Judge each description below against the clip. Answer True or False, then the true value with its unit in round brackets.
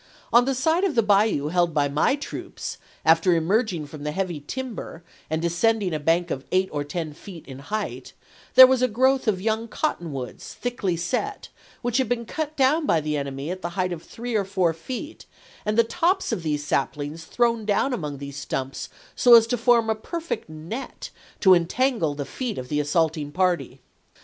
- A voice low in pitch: False (185 Hz)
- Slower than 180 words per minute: False (195 wpm)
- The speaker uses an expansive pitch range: True (7.6 semitones)